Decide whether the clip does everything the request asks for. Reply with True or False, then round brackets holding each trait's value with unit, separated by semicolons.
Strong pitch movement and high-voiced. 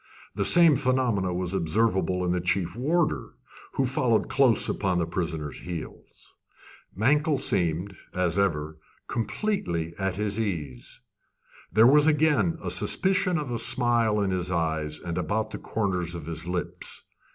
False (6.7 semitones; 95 Hz)